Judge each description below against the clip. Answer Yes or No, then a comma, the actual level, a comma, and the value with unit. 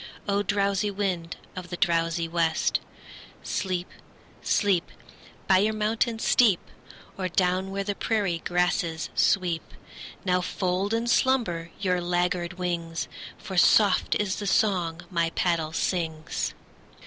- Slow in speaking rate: Yes, slow, 125 wpm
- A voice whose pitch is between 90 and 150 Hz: No, medium, 180 Hz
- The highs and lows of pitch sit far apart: No, average, 2.8 semitones